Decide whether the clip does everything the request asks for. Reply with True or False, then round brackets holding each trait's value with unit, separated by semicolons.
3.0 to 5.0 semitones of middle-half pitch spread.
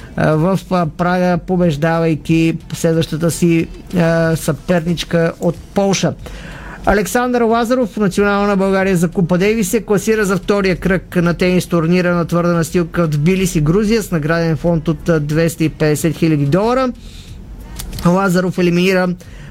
False (2.6 semitones)